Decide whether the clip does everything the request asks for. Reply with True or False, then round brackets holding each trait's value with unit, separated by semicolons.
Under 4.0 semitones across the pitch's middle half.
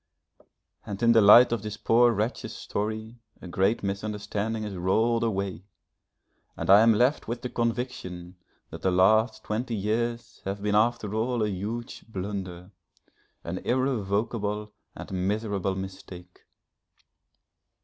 True (3.0 semitones)